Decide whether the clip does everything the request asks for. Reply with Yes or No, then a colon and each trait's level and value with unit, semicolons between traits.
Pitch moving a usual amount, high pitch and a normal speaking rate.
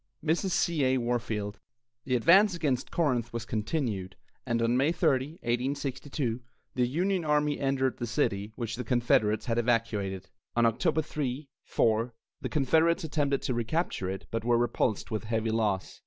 No: average, 4.5 semitones; low, 125 Hz; average, 155 wpm